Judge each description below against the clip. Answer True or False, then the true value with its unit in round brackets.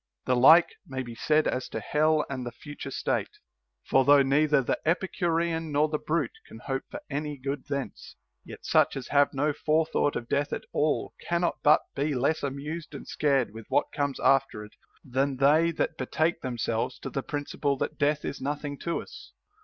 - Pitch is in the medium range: True (145 Hz)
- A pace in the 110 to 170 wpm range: False (190 wpm)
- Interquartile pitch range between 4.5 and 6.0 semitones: False (2.5 semitones)